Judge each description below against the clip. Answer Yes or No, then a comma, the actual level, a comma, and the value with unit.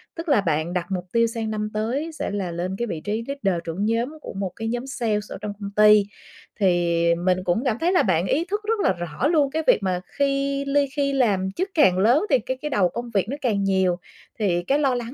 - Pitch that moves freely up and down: Yes, wide, 6.8 semitones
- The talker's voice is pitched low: No, high, 215 Hz